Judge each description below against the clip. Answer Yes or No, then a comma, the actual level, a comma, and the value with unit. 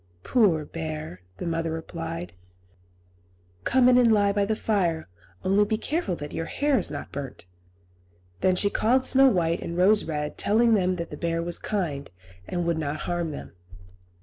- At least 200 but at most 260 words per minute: No, average, 175 wpm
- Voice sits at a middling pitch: Yes, medium, 175 Hz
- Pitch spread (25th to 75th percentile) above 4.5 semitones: Yes, average, 4.9 semitones